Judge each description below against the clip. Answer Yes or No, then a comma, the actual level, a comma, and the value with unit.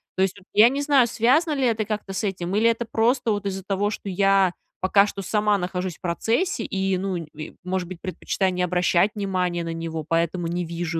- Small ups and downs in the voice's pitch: No, average, 3.1 semitones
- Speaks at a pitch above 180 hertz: Yes, high, 190 Hz